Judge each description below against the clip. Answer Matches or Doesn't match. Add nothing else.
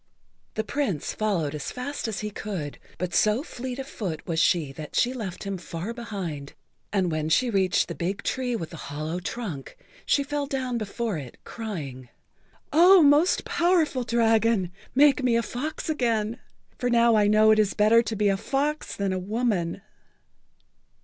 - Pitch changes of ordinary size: Doesn't match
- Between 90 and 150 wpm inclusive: Doesn't match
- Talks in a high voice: Matches